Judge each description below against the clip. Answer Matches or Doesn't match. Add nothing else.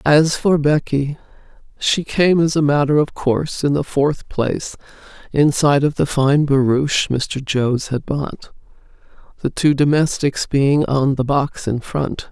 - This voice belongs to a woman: Matches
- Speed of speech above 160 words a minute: Doesn't match